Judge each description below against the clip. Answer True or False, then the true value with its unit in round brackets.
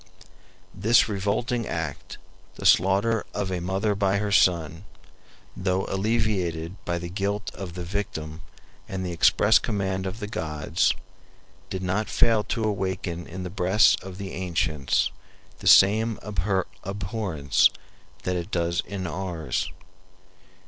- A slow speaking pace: True (130 wpm)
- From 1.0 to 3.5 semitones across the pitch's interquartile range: True (2.8 semitones)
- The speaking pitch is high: False (95 Hz)